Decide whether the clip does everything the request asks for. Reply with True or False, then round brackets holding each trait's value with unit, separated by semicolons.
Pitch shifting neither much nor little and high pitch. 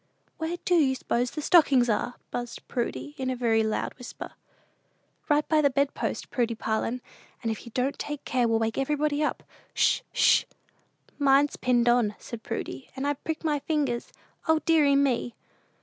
True (3.7 semitones; 265 Hz)